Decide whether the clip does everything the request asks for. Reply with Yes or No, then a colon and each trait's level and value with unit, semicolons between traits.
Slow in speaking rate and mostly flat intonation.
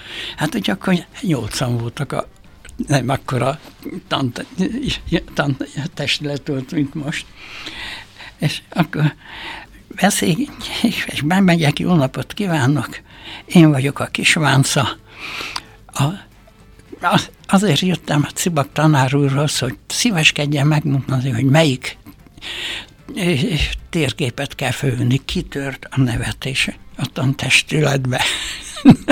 No: slow, 95 wpm; average, 3.1 semitones